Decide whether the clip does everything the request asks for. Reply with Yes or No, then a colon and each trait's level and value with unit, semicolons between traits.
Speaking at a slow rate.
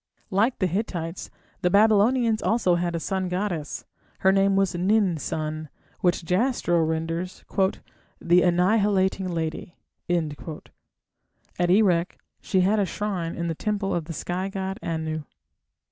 Yes: slow, 130 wpm